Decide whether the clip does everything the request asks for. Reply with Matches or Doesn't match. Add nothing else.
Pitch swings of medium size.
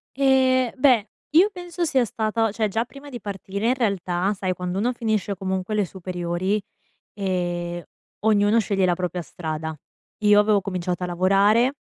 Matches